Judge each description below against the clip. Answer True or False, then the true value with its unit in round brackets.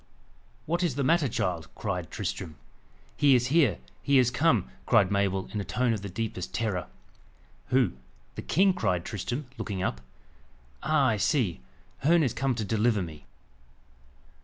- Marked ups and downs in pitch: True (6.2 semitones)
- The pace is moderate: True (160 wpm)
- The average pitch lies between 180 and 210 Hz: False (115 Hz)